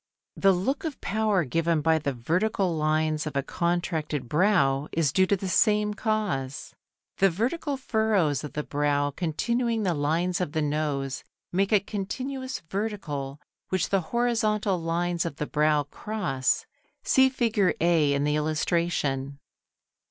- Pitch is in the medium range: Yes, medium, 170 Hz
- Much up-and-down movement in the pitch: Yes, wide, 5.9 semitones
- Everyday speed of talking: Yes, average, 145 wpm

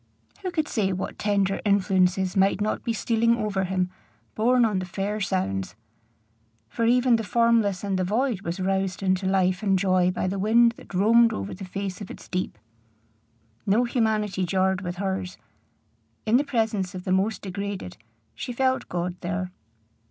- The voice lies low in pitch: No, high, 195 Hz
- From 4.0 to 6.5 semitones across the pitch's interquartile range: No, average, 3.2 semitones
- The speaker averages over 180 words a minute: No, average, 170 wpm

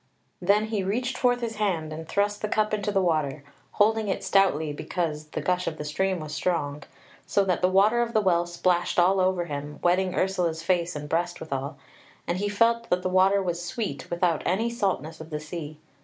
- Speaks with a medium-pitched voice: Yes, medium, 180 Hz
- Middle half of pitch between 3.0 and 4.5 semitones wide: Yes, average, 4.0 semitones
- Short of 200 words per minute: No, fast, 205 wpm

